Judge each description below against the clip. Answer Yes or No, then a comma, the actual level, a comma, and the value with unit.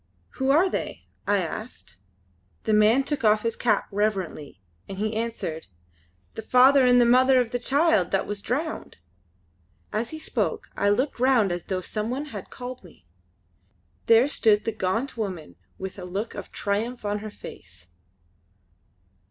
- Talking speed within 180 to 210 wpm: No, average, 160 wpm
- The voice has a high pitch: Yes, high, 220 Hz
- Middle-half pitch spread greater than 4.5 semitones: No, average, 4.2 semitones